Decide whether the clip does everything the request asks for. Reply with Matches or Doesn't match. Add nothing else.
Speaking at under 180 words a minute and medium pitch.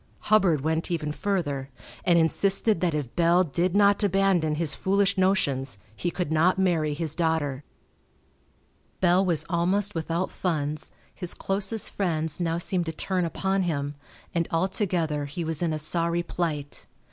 Matches